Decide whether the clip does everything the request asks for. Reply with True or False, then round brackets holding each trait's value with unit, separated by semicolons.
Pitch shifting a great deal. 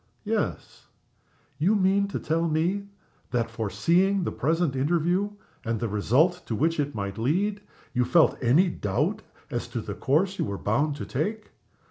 True (7.4 semitones)